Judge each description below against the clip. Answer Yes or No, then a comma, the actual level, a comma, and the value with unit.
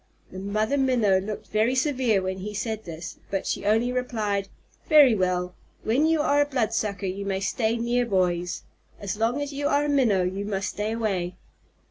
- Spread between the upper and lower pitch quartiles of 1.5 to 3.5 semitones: No, average, 4.5 semitones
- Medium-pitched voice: No, high, 215 Hz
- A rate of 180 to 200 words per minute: Yes, average, 185 wpm